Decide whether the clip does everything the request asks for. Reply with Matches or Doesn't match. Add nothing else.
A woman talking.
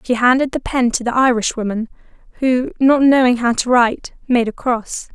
Matches